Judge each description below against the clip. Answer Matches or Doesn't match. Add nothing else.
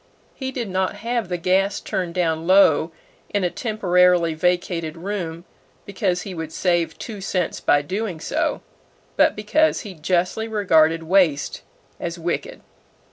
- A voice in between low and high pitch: Matches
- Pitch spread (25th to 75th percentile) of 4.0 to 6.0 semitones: Doesn't match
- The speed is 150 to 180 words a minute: Doesn't match